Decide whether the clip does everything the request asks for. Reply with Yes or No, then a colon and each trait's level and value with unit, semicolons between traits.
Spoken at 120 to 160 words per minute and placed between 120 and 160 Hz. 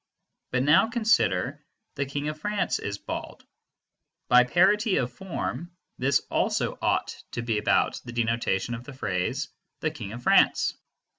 Yes: average, 150 wpm; low, 135 Hz